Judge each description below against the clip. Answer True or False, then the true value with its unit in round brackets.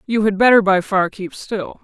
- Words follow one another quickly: True (230 wpm)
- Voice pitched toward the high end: True (205 Hz)